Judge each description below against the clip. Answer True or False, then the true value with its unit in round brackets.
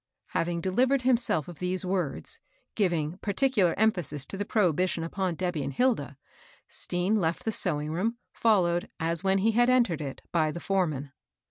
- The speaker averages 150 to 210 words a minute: True (160 wpm)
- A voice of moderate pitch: True (180 Hz)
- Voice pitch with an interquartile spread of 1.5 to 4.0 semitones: False (4.5 semitones)